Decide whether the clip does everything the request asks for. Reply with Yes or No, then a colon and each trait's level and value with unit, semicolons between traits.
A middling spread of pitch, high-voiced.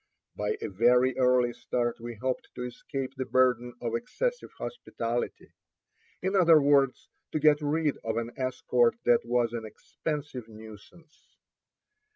No: average, 3.7 semitones; low, 125 Hz